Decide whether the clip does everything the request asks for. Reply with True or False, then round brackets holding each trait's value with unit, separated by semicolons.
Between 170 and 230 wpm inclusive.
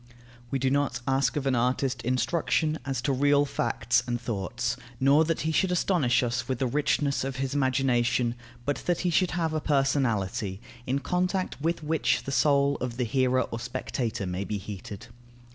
True (180 wpm)